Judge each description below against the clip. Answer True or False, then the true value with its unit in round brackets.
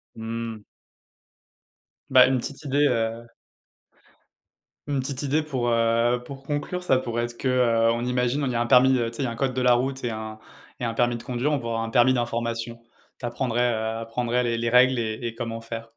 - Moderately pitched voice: False (120 Hz)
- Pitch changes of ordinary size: False (2.0 semitones)